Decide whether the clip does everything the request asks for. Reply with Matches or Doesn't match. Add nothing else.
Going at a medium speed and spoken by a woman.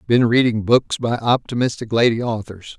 Doesn't match